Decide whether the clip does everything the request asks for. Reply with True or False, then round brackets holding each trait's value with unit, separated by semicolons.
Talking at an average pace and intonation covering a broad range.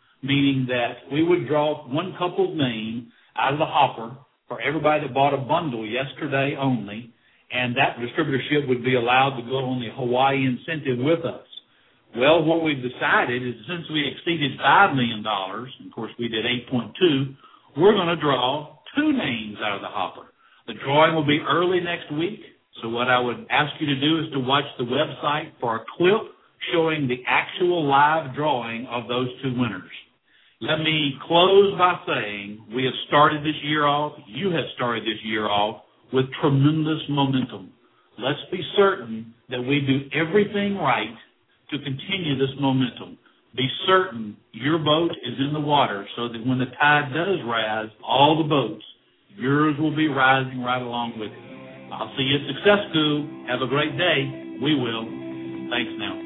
False (175 wpm; 4.1 semitones)